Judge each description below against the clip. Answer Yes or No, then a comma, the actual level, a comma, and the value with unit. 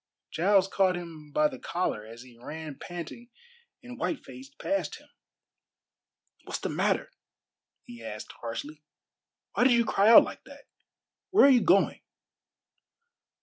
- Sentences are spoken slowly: No, average, 145 wpm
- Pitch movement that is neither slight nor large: No, wide, 8.2 semitones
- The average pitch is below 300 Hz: Yes, medium, 185 Hz